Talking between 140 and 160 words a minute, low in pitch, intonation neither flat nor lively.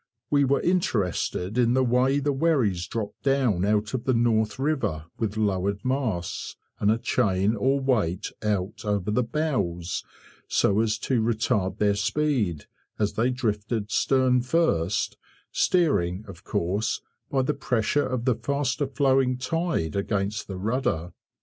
Yes: average, 145 wpm; low, 115 Hz; average, 4.7 semitones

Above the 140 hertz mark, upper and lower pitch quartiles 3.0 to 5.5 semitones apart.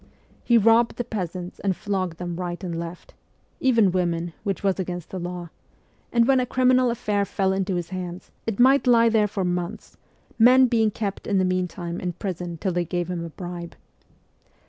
Yes: medium, 185 Hz; average, 4.1 semitones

